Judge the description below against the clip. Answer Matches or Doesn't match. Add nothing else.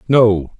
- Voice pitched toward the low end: Matches